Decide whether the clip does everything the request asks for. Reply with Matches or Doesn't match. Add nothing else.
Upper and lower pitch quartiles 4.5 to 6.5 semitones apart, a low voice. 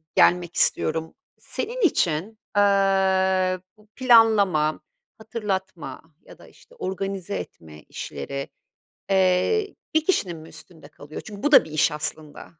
Doesn't match